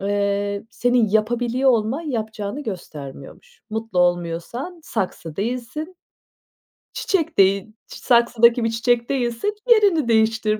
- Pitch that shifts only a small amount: No, average, 3.6 semitones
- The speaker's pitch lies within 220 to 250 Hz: Yes, high, 225 Hz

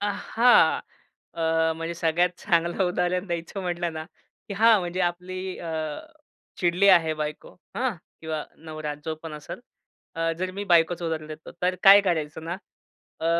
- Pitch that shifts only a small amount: Yes, narrow, 2.3 semitones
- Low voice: No, medium, 170 Hz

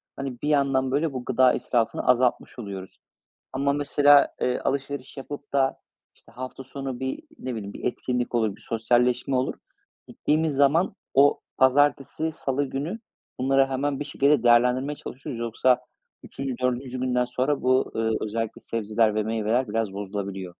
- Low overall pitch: Yes, low, 130 Hz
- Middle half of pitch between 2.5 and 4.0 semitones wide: Yes, average, 2.9 semitones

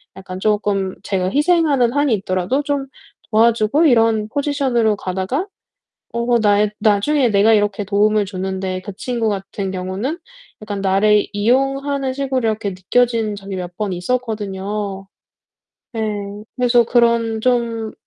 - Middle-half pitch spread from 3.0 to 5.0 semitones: Yes, average, 3.9 semitones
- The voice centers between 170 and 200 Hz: No, high, 215 Hz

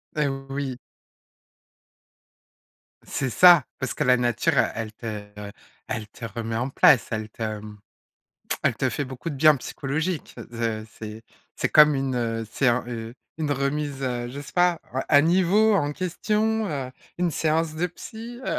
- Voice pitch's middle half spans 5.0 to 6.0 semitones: Yes, wide, 5.5 semitones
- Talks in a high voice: No, low, 135 Hz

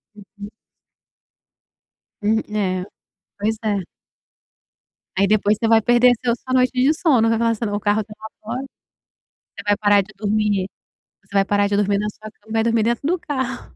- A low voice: No, high, 215 Hz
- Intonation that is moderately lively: No, narrow, 2.3 semitones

